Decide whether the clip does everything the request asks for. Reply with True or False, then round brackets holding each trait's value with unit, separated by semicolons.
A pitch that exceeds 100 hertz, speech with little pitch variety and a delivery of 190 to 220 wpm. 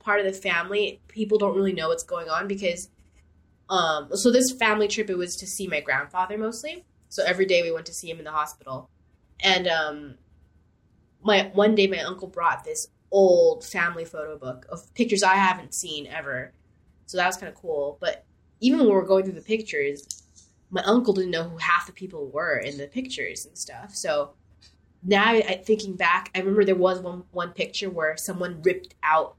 False (185 Hz; 4.6 semitones; 200 wpm)